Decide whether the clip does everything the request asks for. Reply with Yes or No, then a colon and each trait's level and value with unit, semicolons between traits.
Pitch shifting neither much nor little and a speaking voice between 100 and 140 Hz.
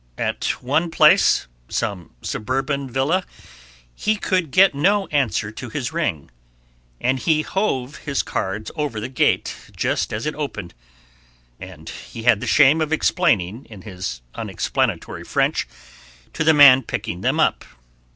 No: wide, 6.4 semitones; low, 135 Hz